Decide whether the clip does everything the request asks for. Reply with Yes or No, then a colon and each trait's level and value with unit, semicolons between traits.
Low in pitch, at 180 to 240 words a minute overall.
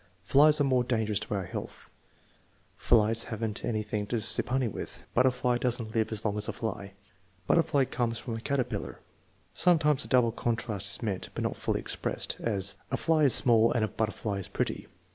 Yes: low, 115 Hz; average, 200 wpm